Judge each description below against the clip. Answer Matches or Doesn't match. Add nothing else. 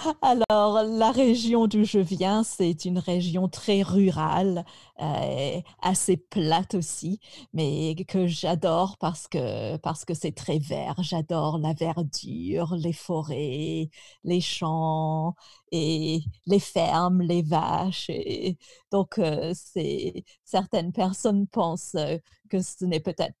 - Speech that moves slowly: Matches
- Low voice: Doesn't match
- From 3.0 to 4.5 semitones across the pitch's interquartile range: Matches